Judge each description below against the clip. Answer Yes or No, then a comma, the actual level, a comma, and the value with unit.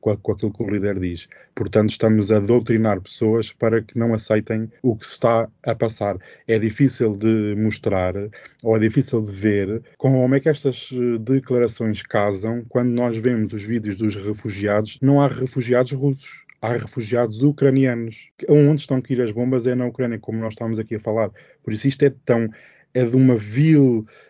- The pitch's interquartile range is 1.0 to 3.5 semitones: Yes, average, 2.7 semitones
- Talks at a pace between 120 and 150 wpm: No, fast, 185 wpm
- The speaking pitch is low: Yes, low, 115 Hz